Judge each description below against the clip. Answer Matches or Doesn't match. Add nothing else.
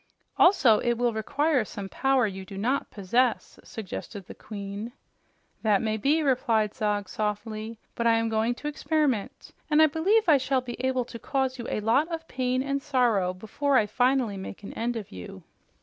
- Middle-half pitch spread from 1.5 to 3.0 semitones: Doesn't match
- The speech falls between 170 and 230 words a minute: Matches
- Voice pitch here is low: Doesn't match